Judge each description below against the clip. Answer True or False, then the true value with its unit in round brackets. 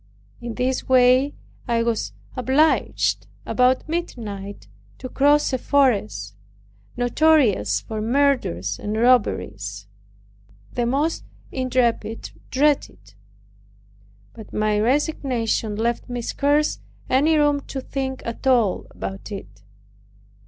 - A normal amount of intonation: True (4.5 semitones)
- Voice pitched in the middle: False (245 Hz)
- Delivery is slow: True (105 wpm)